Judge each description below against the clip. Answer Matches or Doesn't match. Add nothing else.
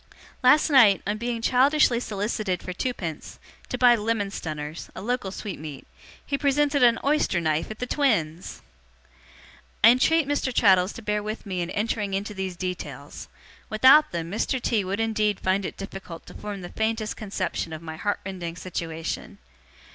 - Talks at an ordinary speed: Matches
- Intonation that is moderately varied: Matches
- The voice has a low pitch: Doesn't match